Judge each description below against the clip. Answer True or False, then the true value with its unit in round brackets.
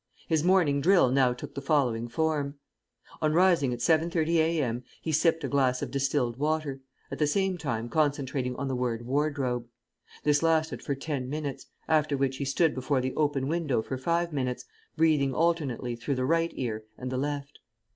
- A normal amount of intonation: True (3.6 semitones)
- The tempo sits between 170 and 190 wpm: True (180 wpm)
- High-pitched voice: False (140 Hz)